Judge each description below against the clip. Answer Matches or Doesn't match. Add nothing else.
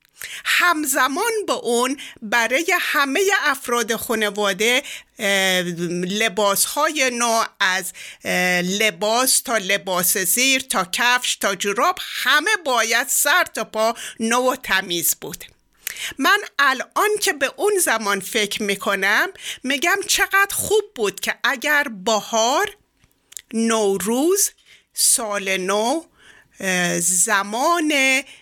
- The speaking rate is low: Matches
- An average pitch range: Doesn't match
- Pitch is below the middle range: Doesn't match